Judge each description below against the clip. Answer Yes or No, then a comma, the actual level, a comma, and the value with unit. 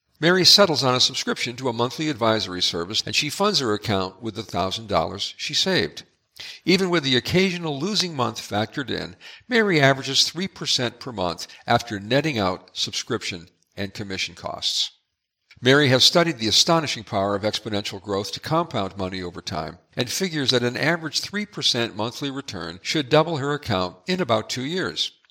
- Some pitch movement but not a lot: No, wide, 7.2 semitones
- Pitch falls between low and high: No, low, 120 Hz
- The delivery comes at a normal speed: Yes, average, 165 wpm